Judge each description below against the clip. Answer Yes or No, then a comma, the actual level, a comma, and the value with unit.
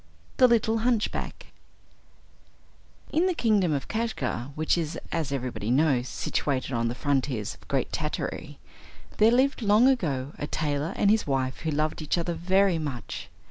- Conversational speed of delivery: Yes, average, 155 wpm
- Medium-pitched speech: Yes, medium, 155 Hz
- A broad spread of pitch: Yes, wide, 7.9 semitones